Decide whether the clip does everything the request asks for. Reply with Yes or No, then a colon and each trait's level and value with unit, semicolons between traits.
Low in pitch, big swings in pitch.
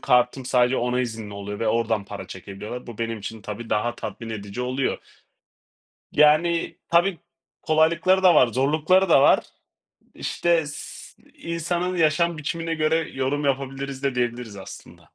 Yes: low, 130 Hz; wide, 5.8 semitones